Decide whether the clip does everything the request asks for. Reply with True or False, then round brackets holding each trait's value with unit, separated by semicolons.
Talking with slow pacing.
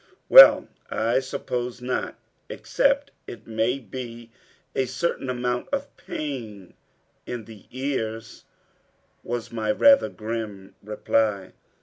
True (105 wpm)